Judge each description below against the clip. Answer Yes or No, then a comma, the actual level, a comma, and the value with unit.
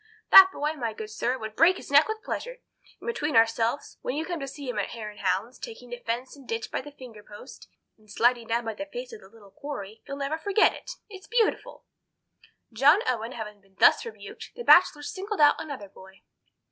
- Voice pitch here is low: No, very high, 255 Hz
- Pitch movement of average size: No, wide, 6.0 semitones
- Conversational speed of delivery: No, fast, 215 wpm